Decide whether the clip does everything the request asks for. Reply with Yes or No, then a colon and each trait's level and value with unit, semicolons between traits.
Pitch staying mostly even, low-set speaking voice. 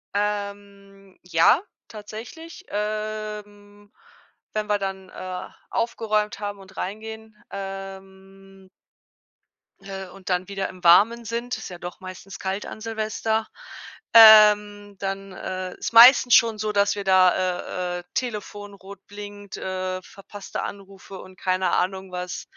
No: narrow, 1.9 semitones; high, 200 Hz